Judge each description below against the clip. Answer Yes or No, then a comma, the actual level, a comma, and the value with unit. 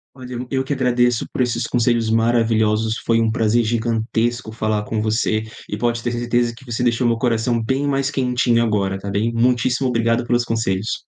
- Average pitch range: No, narrow, 1.7 semitones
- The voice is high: No, low, 115 Hz